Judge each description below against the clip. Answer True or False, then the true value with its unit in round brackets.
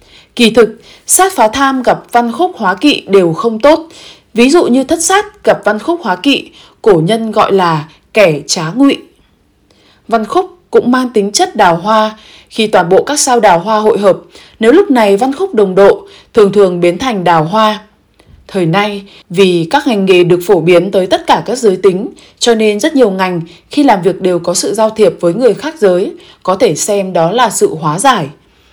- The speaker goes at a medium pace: True (210 wpm)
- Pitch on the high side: True (215 Hz)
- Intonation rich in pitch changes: True (7.0 semitones)